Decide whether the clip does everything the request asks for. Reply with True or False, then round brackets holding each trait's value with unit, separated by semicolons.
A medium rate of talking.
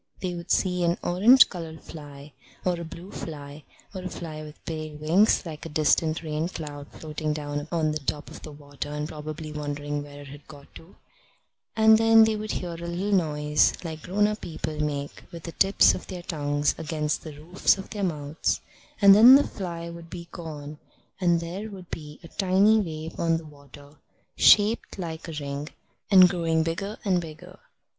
True (190 wpm)